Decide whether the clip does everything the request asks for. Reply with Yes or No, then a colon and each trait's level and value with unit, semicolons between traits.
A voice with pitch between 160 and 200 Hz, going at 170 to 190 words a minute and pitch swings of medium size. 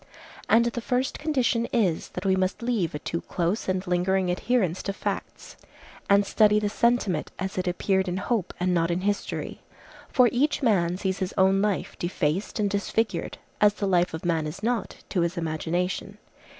Yes: high, 190 Hz; average, 180 wpm; average, 3.3 semitones